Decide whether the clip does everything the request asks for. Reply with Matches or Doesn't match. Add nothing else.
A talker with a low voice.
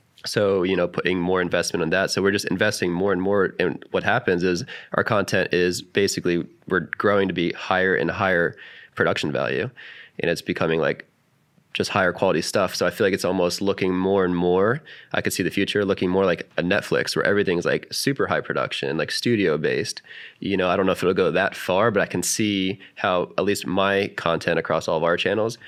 Matches